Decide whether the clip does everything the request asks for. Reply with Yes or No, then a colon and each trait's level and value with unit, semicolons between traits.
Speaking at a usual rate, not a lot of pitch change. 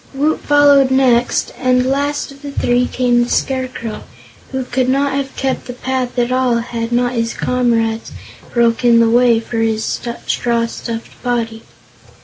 Yes: average, 155 wpm; narrow, 2.0 semitones